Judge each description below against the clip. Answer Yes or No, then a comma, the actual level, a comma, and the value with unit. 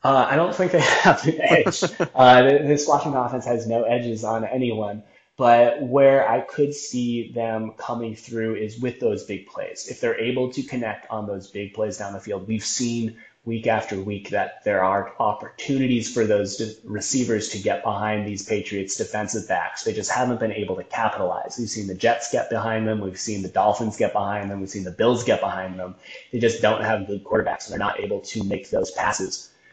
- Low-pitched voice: Yes, low, 115 Hz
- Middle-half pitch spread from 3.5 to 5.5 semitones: No, average, 3.0 semitones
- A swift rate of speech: Yes, fast, 210 wpm